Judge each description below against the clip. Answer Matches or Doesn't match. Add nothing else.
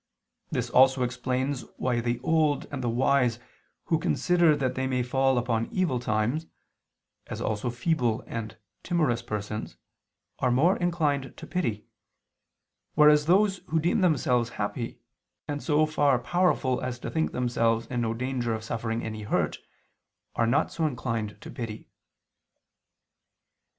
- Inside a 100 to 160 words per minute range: Matches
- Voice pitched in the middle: Doesn't match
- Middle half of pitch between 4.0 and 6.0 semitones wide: Matches